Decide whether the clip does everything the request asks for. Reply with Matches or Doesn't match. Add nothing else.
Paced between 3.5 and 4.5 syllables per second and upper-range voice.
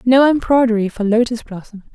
Doesn't match